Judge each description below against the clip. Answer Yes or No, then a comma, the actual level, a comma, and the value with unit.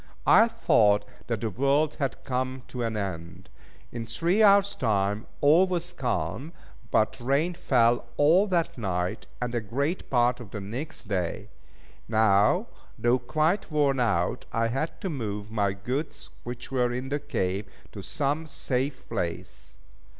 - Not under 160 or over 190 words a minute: No, average, 150 wpm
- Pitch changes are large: Yes, wide, 5.7 semitones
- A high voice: No, low, 125 Hz